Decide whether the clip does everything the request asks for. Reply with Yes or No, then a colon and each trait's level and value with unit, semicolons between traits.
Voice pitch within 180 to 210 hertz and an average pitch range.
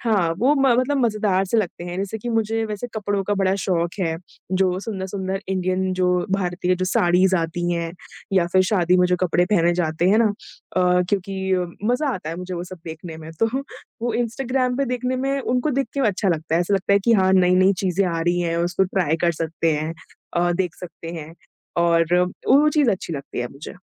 Yes: medium, 185 Hz; average, 3.5 semitones